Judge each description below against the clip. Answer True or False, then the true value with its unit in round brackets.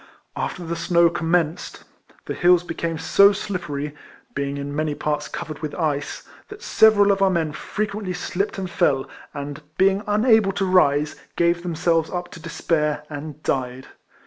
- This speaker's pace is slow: False (155 wpm)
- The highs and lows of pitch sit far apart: False (4.0 semitones)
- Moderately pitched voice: True (170 Hz)